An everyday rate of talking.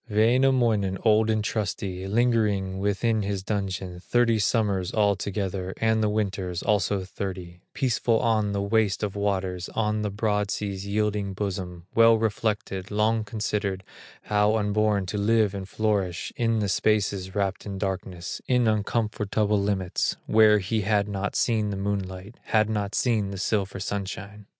Yes: average, 145 wpm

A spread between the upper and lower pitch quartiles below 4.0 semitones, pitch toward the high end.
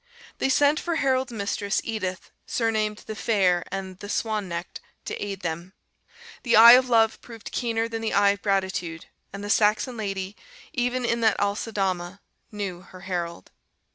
Yes: average, 3.3 semitones; high, 205 Hz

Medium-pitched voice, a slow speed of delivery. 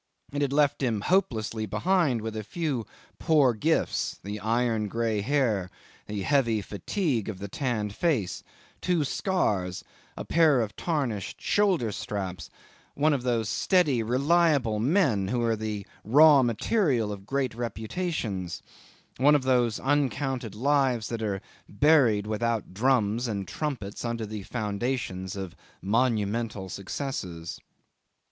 No: low, 115 Hz; slow, 130 wpm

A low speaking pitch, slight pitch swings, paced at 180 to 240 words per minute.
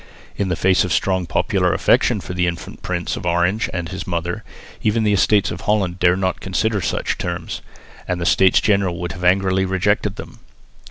Yes: very low, 95 Hz; narrow, 1.7 semitones; average, 200 wpm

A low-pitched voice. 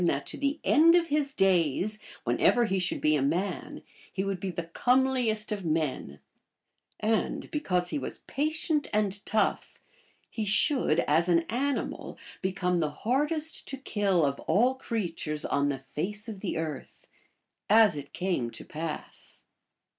No: high, 195 Hz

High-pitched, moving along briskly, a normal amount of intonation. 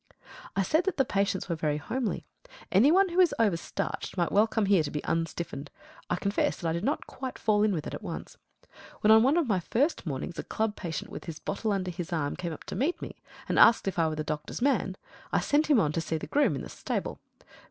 No: high, 195 Hz; fast, 250 wpm; wide, 6.5 semitones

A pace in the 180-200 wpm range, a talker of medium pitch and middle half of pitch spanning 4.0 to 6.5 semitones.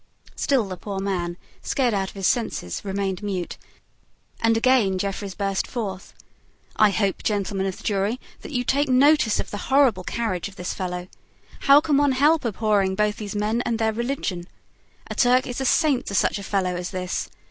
No: average, 190 wpm; high, 210 Hz; average, 4.4 semitones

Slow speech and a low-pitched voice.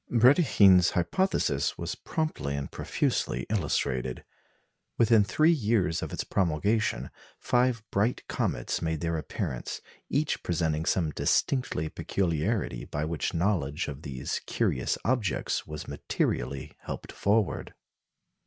Yes: slow, 115 wpm; very low, 90 Hz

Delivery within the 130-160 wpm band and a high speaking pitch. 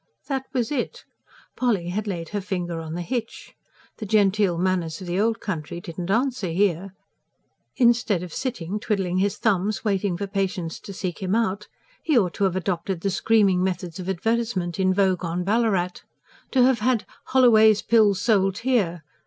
No: average, 175 wpm; high, 195 Hz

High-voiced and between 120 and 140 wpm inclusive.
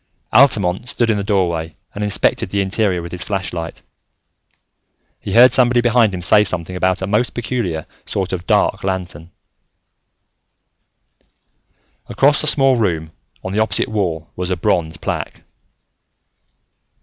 No: very low, 95 Hz; slow, 135 wpm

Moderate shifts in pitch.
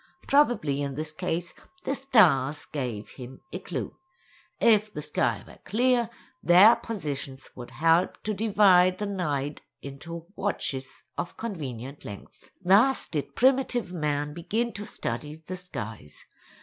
No: wide, 7.0 semitones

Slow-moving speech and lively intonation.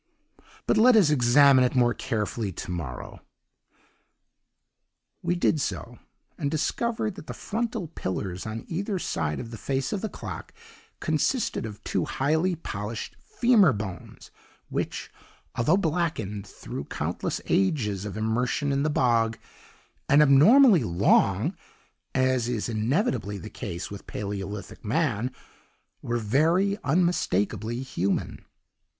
Yes: slow, 125 wpm; wide, 8.1 semitones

